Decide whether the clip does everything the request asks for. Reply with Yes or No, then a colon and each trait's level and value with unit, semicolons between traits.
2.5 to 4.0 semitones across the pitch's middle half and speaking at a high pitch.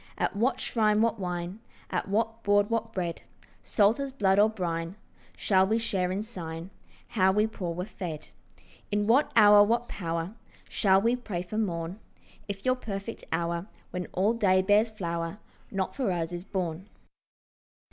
Yes: average, 3.7 semitones; high, 200 Hz